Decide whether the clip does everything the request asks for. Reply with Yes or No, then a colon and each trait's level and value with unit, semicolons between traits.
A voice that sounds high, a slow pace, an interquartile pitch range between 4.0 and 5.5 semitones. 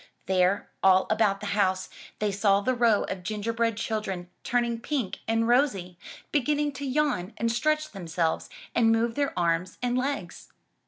No: high, 225 Hz; average, 155 wpm; average, 4.5 semitones